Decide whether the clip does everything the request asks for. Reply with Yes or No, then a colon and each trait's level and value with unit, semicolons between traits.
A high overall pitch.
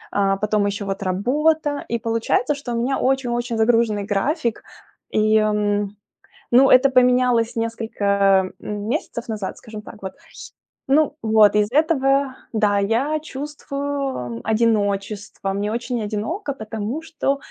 Yes: high, 230 Hz